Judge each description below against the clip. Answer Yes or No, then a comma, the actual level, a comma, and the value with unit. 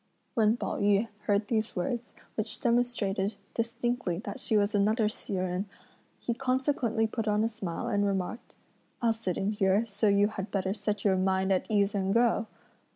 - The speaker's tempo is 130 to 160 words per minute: No, average, 175 wpm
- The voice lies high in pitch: Yes, high, 210 Hz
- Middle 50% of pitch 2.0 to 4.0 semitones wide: Yes, average, 2.7 semitones